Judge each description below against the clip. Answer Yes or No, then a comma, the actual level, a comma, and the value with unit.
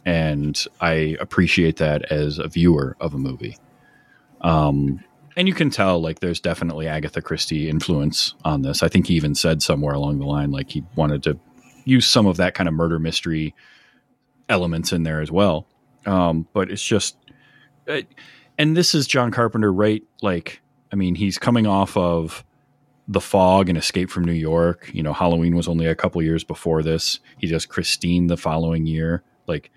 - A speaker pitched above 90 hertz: No, very low, 85 Hz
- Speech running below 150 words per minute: No, average, 185 wpm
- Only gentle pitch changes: No, average, 3.4 semitones